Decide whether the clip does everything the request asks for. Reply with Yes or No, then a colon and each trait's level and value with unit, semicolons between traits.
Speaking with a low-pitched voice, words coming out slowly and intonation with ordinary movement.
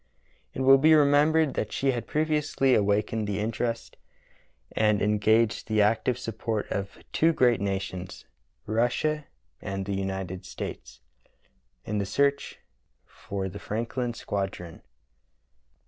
Yes: low, 110 Hz; slow, 130 wpm; average, 4.9 semitones